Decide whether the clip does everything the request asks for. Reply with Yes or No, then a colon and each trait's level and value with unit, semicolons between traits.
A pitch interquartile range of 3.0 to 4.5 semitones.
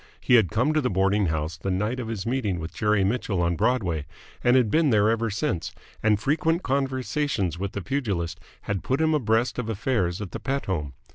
No: wide, 5.4 semitones